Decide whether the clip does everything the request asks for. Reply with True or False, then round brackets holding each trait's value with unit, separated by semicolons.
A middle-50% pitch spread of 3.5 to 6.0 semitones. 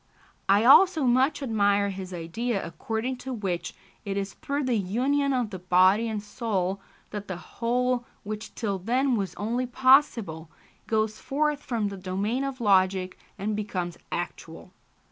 True (4.7 semitones)